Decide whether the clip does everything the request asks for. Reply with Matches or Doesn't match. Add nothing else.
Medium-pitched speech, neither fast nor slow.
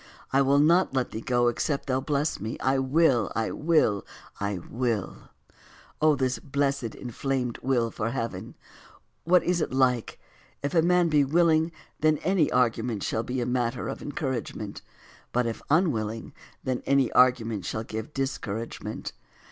Doesn't match